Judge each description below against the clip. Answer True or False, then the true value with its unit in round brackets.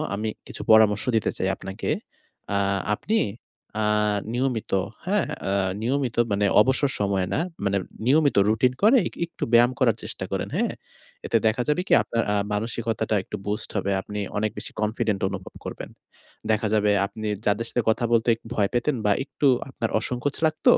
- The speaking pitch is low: True (110 Hz)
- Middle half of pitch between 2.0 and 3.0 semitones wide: False (3.6 semitones)